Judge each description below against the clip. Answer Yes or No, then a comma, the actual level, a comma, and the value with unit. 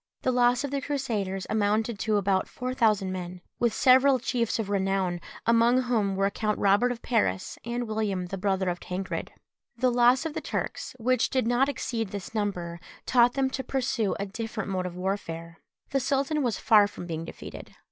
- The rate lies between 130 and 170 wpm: No, average, 190 wpm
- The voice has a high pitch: Yes, high, 220 Hz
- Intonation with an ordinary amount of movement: Yes, average, 4.4 semitones